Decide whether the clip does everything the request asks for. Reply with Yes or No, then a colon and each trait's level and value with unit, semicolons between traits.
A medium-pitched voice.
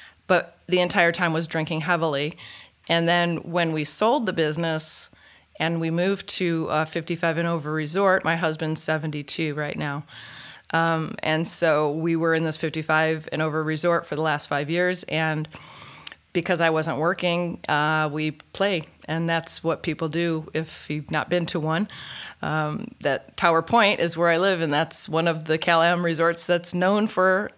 Yes: medium, 165 Hz